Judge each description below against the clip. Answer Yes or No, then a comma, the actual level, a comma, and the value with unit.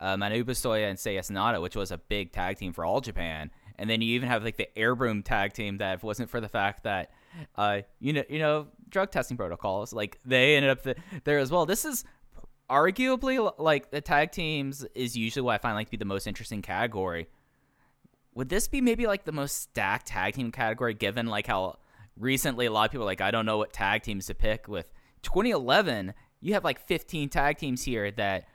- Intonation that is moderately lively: No, wide, 5.7 semitones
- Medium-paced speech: No, fast, 225 wpm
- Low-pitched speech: Yes, low, 120 Hz